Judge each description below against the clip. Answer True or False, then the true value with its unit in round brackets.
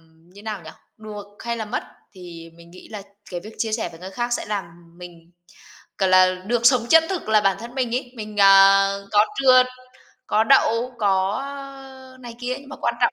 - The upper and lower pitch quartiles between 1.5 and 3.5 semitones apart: False (4.1 semitones)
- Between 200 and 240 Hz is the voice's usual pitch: True (210 Hz)